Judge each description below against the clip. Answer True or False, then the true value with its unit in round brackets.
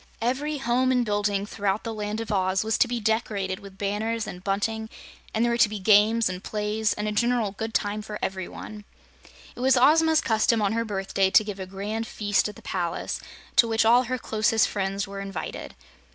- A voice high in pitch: True (215 Hz)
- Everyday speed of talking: False (210 wpm)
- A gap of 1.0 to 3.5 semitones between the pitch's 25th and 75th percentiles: True (2.5 semitones)